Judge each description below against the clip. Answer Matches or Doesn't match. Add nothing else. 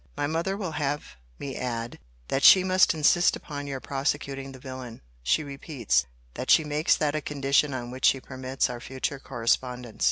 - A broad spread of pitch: Doesn't match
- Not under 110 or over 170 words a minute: Doesn't match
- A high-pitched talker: Doesn't match